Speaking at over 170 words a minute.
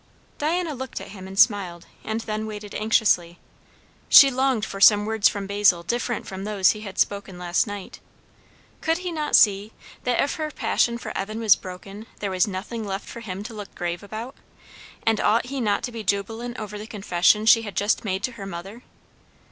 Yes: average, 195 wpm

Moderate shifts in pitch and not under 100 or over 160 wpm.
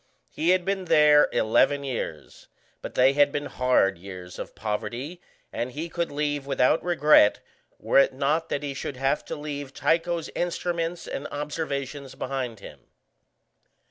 Yes: average, 3.9 semitones; average, 150 wpm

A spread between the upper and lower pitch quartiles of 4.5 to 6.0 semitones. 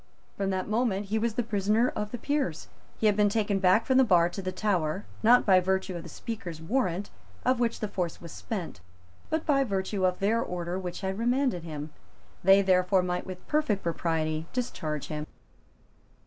No: average, 4.1 semitones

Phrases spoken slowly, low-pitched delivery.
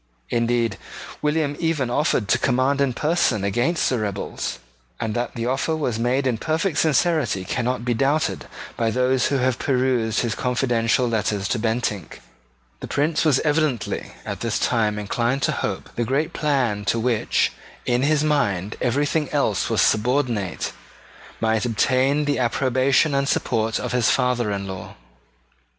No: average, 155 wpm; low, 125 Hz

